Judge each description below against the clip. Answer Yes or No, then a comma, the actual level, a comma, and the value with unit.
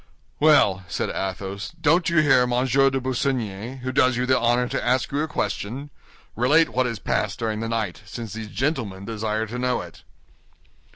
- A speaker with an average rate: Yes, average, 180 wpm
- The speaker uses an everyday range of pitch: Yes, average, 3.7 semitones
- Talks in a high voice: No, low, 125 Hz